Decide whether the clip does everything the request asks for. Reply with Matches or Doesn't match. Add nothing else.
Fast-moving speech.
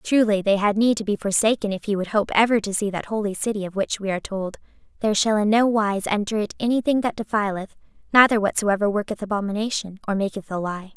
Matches